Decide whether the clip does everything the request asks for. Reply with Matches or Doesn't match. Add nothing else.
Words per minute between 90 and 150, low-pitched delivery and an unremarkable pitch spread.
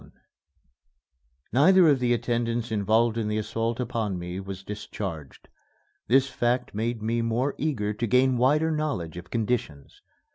Matches